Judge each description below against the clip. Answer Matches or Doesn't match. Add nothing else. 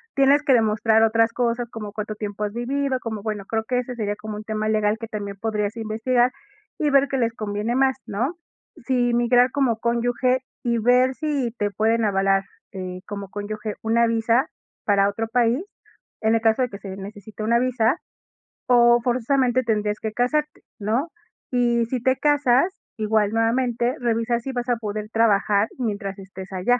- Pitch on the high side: Matches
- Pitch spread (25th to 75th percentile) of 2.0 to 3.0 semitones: Matches